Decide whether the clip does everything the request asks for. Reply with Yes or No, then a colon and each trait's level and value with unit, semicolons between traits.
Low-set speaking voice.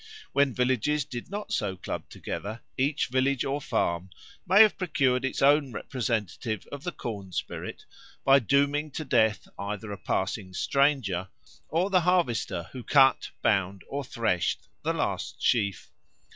Yes: low, 130 Hz